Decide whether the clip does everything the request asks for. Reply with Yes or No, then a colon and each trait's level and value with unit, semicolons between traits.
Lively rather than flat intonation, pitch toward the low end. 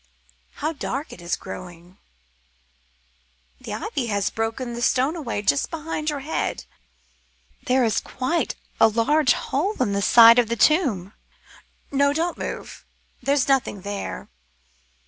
No: wide, 5.8 semitones; very high, 250 Hz